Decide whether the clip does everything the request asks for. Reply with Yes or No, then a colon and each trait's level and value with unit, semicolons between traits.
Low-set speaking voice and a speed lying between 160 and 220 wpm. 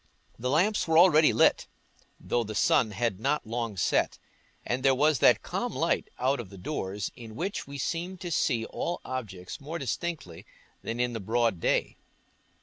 Yes: low, 125 Hz; average, 170 wpm